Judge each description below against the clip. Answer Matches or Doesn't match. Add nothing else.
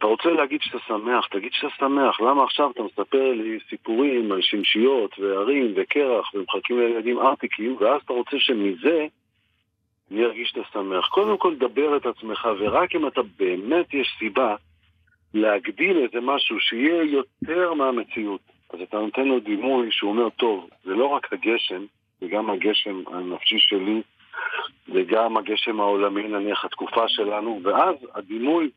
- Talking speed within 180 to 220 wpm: Doesn't match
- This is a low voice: Matches